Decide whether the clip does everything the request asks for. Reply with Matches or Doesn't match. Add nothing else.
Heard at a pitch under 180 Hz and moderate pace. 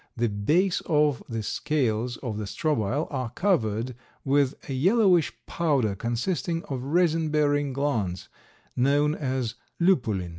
Doesn't match